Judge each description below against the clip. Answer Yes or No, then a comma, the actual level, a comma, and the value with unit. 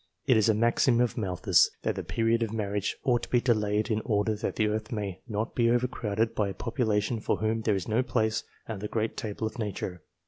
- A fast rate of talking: Yes, fast, 230 wpm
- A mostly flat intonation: Yes, narrow, 1.9 semitones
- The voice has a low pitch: Yes, low, 110 Hz